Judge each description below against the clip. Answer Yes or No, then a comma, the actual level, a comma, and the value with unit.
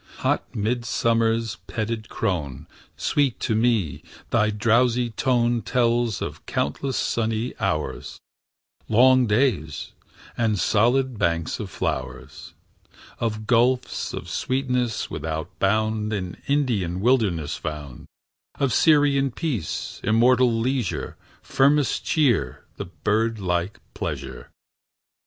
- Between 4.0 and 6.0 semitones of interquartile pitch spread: Yes, average, 4.3 semitones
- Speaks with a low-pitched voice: Yes, low, 115 Hz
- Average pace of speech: No, slow, 100 wpm